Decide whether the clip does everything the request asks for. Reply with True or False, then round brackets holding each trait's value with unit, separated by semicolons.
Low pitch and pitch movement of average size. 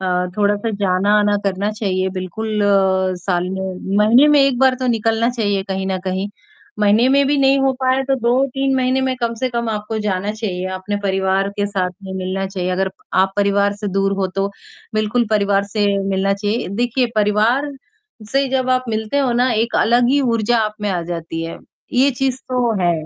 False (210 Hz; 4.2 semitones)